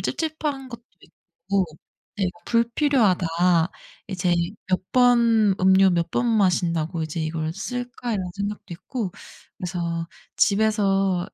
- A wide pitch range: No, average, 4.9 semitones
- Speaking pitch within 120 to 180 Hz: No, high, 195 Hz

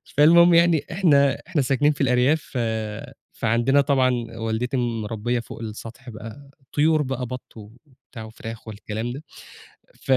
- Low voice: Yes, low, 125 Hz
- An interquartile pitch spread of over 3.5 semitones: Yes, average, 3.9 semitones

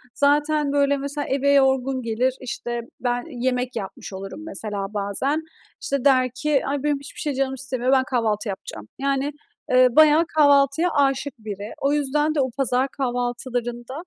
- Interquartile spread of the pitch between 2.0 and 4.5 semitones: Yes, average, 2.7 semitones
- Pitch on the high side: Yes, very high, 265 Hz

